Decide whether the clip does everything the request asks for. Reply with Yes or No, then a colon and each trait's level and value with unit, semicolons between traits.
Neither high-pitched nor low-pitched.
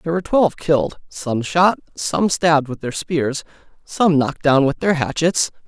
Yes: medium, 155 Hz